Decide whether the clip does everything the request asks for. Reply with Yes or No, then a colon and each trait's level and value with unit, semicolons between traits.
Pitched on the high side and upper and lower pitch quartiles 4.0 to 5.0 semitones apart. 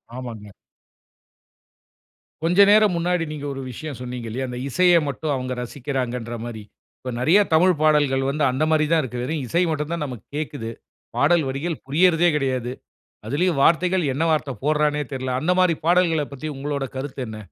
No: medium, 145 Hz; average, 4.3 semitones